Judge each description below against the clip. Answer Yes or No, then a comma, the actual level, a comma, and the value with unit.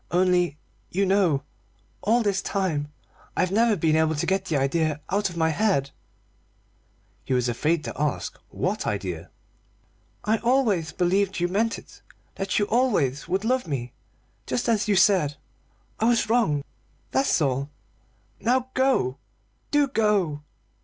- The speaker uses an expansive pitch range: Yes, wide, 6.4 semitones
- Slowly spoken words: No, average, 145 wpm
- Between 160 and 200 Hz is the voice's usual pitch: Yes, medium, 185 Hz